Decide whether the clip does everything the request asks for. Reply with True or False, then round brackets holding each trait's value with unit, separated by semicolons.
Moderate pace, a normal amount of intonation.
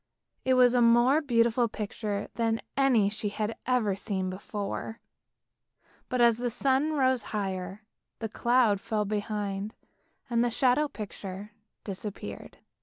False (130 wpm; 3.3 semitones)